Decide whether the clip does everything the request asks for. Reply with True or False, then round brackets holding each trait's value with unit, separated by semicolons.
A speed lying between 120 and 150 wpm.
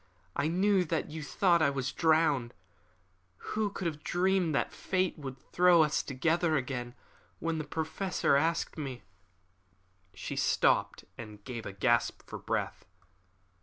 True (145 wpm)